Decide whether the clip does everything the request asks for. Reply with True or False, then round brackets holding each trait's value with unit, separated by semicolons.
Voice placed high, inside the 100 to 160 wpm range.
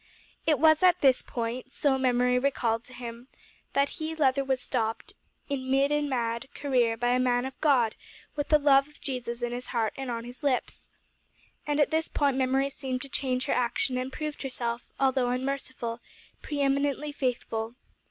False (260 Hz; 180 wpm)